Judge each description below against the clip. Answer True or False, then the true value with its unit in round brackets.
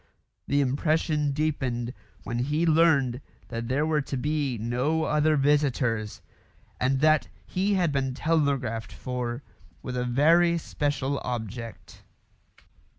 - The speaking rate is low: True (120 wpm)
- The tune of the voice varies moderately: True (3.7 semitones)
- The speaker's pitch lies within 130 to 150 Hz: True (140 Hz)